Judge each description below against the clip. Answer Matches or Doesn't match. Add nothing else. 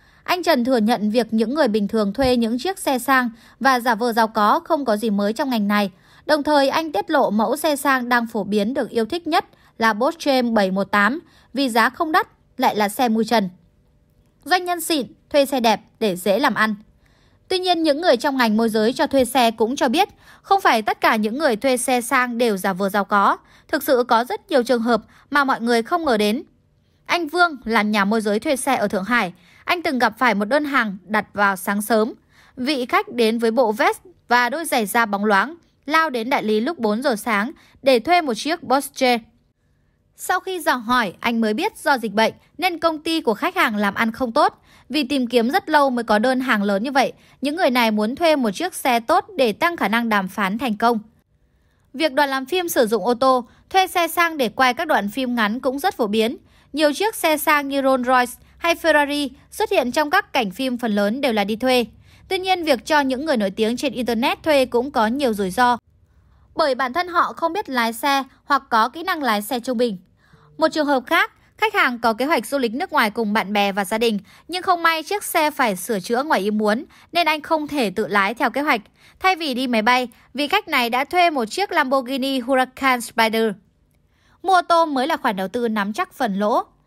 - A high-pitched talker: Matches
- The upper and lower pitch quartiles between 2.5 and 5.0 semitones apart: Doesn't match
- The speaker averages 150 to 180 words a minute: Doesn't match